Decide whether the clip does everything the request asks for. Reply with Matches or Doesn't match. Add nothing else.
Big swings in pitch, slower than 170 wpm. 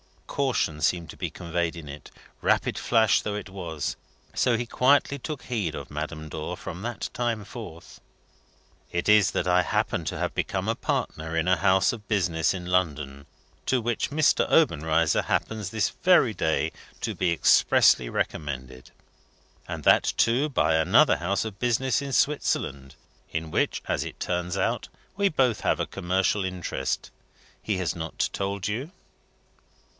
Matches